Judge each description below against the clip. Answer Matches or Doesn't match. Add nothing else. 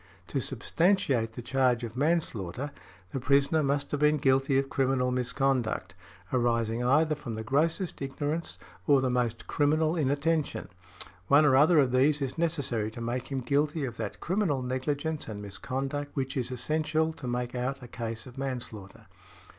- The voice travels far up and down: Doesn't match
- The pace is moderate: Matches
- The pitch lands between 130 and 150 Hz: Matches